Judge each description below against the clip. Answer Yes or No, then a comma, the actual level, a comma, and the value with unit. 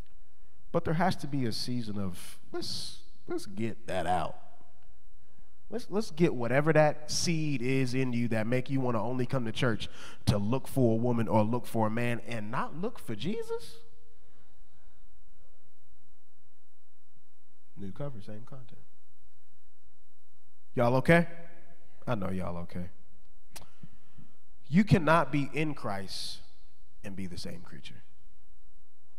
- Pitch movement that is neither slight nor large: No, wide, 6.5 semitones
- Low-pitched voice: Yes, low, 120 Hz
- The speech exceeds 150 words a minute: No, slow, 135 wpm